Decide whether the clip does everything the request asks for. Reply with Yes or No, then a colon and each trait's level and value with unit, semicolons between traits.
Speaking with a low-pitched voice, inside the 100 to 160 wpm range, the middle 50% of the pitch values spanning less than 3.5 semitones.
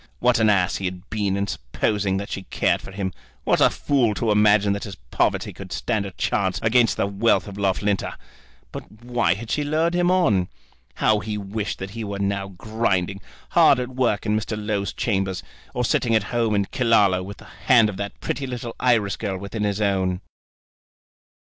No: low, 105 Hz; average, 195 wpm; average, 2.8 semitones